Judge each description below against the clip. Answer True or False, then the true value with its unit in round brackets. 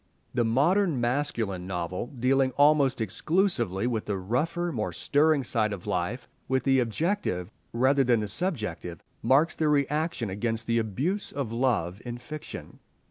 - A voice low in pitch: True (125 Hz)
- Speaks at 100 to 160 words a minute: True (145 wpm)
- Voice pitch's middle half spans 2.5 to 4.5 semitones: False (5.2 semitones)